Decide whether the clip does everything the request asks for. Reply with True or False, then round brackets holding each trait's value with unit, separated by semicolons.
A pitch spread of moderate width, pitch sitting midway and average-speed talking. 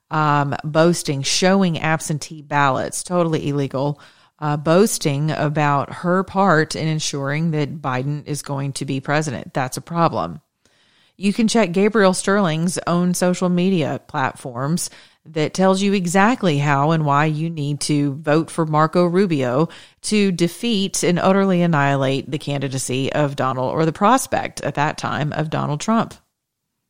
True (3.9 semitones; 155 Hz; 145 wpm)